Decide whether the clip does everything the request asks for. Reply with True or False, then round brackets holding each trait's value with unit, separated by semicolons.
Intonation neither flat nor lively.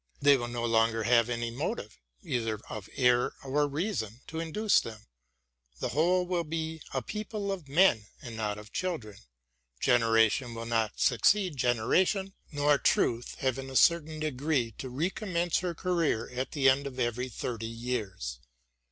False (5.9 semitones)